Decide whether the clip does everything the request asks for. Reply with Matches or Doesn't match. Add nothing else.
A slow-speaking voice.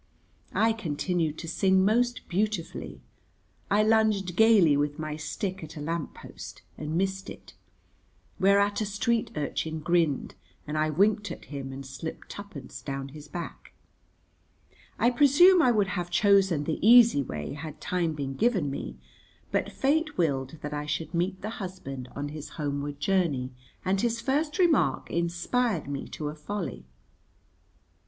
Doesn't match